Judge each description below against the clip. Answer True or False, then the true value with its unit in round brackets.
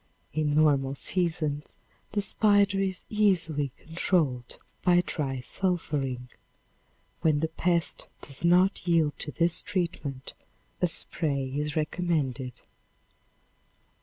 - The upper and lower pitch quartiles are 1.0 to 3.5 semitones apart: False (4.0 semitones)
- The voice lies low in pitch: False (160 Hz)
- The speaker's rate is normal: False (105 wpm)